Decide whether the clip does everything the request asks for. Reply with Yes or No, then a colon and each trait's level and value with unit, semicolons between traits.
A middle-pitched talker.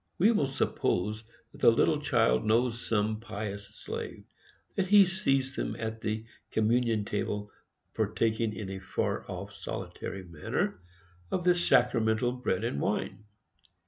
No: low, 110 Hz